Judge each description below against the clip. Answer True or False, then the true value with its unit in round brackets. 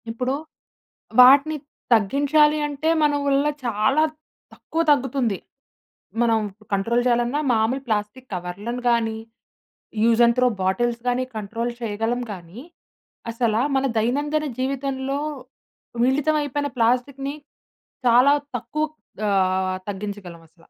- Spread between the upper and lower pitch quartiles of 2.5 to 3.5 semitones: False (4.3 semitones)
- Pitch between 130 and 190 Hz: False (240 Hz)